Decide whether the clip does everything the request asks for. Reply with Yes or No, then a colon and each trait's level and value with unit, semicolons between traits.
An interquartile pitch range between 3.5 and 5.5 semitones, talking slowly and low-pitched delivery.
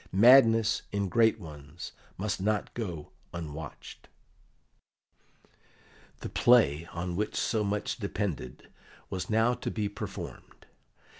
Yes: average, 4.8 semitones; slow, 105 wpm; low, 100 Hz